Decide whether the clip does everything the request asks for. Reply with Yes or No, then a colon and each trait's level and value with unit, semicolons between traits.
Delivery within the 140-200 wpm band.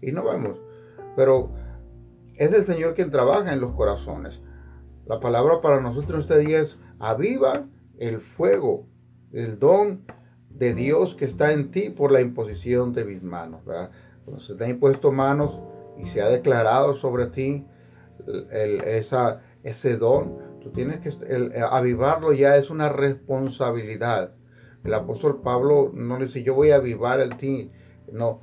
Yes: average, 160 wpm